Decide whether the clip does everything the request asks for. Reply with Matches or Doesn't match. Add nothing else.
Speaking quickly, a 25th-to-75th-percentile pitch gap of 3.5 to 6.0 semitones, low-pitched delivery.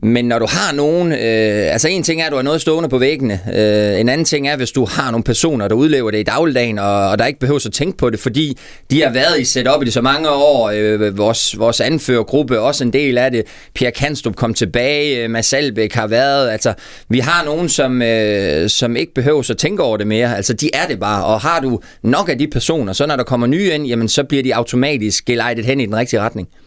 Matches